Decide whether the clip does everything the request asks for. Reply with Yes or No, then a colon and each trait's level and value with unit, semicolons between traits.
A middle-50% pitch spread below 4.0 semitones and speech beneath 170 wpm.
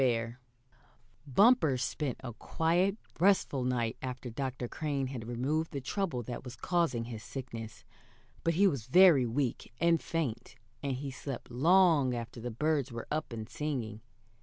No: average, 4.9 semitones; average, 155 wpm